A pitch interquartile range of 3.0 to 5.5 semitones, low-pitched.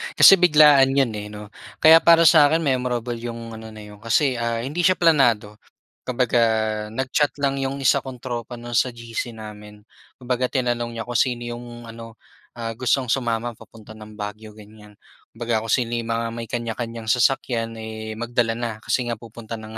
No: narrow, 2.4 semitones; low, 120 Hz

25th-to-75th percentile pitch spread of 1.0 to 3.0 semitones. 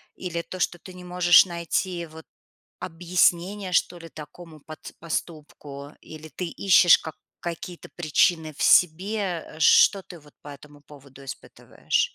Yes: narrow, 2.6 semitones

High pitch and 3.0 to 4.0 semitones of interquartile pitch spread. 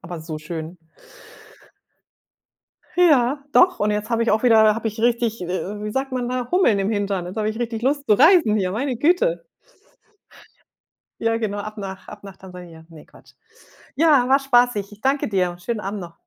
No: high, 220 Hz; average, 4.5 semitones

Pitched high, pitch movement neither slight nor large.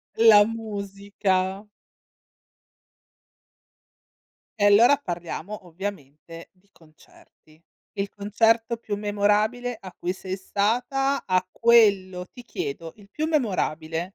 Yes: high, 200 Hz; average, 3.5 semitones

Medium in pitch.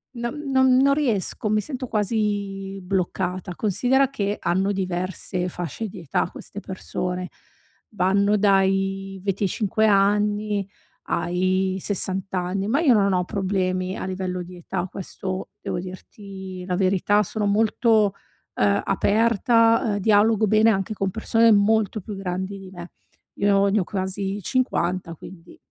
No: high, 195 Hz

